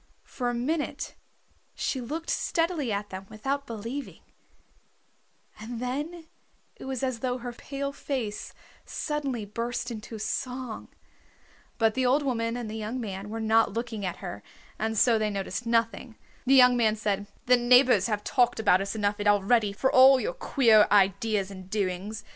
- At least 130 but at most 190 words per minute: Yes, average, 160 wpm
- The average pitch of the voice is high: Yes, high, 230 Hz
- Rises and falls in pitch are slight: No, average, 3.6 semitones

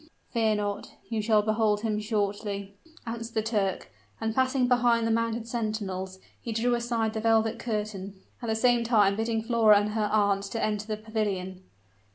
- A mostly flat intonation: Yes, narrow, 1.8 semitones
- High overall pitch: Yes, high, 220 Hz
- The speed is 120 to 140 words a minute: No, average, 170 wpm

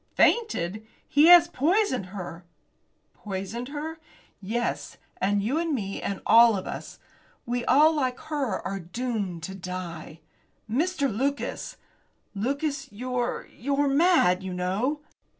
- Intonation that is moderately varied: No, wide, 7.0 semitones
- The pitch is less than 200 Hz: No, high, 240 Hz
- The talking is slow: Yes, slow, 125 wpm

